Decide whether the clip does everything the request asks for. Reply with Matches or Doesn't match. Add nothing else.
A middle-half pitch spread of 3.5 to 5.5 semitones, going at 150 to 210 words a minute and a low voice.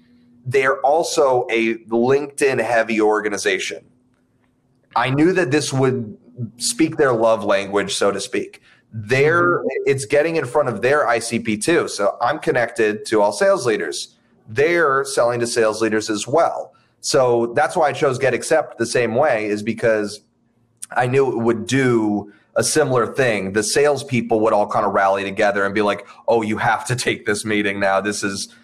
Matches